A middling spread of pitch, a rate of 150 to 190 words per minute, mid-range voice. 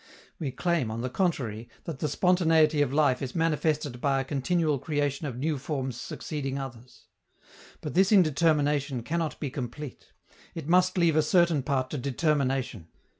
Yes: average, 3.7 semitones; average, 160 wpm; medium, 145 Hz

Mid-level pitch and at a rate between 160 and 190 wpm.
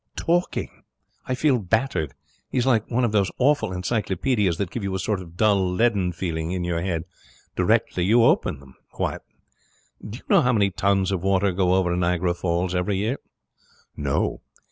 No: very low, 95 Hz; average, 170 wpm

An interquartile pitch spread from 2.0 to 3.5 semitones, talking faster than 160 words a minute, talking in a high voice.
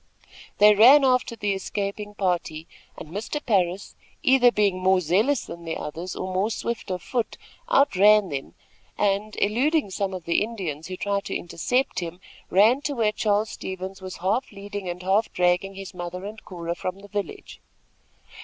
Yes: average, 2.9 semitones; average, 170 wpm; high, 200 Hz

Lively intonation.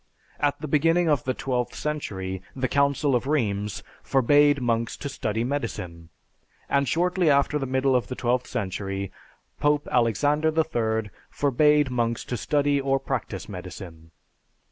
No: average, 4.5 semitones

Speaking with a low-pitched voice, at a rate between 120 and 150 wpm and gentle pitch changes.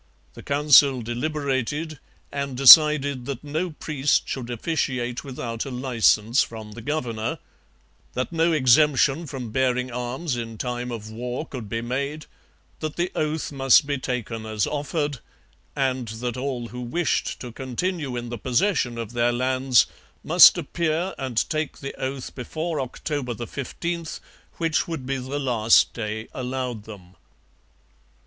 No: low, 130 Hz; average, 140 wpm; average, 3.6 semitones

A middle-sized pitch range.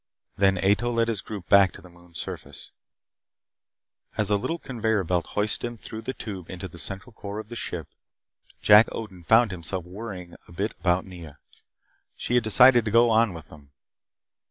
Yes: average, 4.2 semitones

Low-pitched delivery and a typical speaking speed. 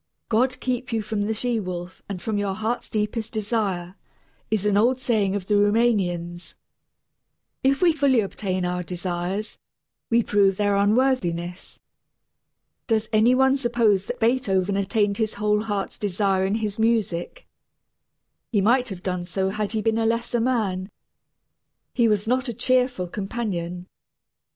No: high, 210 Hz; average, 150 wpm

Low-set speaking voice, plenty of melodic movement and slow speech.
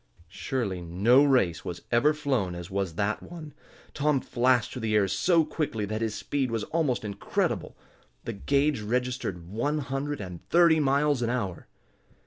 No: low, 120 Hz; wide, 6.2 semitones; average, 160 wpm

